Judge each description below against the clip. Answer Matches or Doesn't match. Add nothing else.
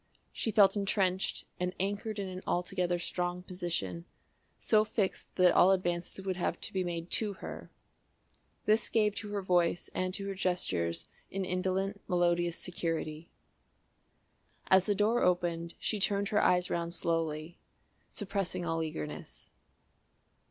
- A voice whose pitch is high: Doesn't match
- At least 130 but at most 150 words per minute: Matches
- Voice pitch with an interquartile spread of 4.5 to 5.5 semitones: Doesn't match